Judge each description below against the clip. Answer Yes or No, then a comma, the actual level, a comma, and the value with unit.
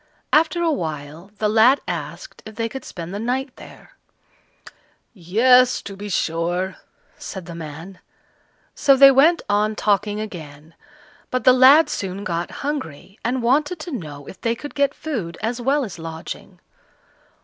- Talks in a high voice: Yes, high, 215 Hz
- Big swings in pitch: Yes, wide, 7.2 semitones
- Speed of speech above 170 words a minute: No, average, 155 wpm